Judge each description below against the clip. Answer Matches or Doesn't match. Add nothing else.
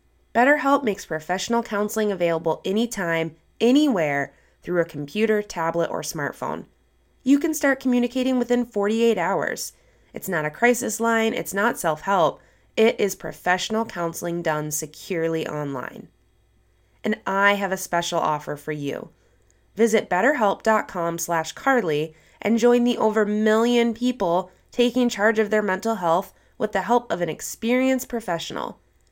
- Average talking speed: Doesn't match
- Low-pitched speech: Doesn't match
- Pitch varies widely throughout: Matches